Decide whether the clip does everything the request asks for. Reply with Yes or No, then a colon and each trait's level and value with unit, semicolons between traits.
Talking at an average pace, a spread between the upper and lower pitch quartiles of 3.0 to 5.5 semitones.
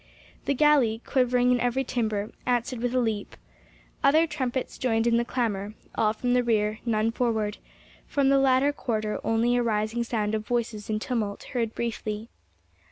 No: average, 160 wpm; narrow, 2.5 semitones